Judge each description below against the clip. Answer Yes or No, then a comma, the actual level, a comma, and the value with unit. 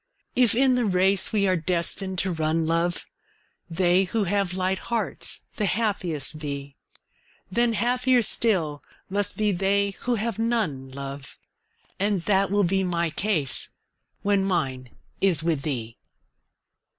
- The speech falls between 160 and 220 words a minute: No, average, 140 wpm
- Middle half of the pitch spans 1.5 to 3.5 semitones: No, average, 4.3 semitones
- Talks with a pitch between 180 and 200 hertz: Yes, high, 190 Hz